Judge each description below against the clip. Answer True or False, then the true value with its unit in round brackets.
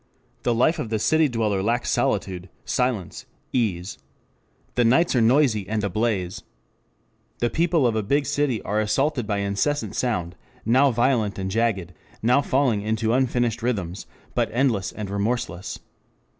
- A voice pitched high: False (115 Hz)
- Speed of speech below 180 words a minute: True (145 wpm)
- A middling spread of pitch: True (4.0 semitones)